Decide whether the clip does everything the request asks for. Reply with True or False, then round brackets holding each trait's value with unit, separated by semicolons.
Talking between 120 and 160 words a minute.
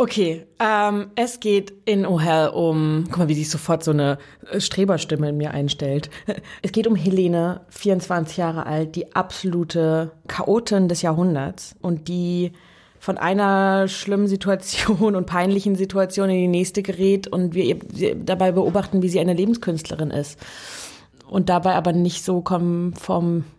True (155 wpm)